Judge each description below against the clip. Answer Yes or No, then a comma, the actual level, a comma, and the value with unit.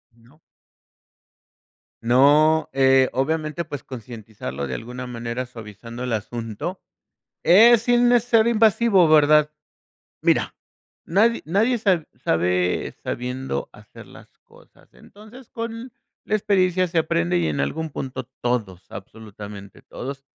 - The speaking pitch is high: No, low, 135 Hz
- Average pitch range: No, wide, 8.5 semitones